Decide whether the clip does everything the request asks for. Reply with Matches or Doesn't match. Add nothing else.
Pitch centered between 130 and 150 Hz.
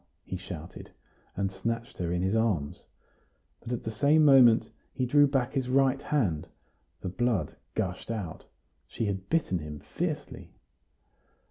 Doesn't match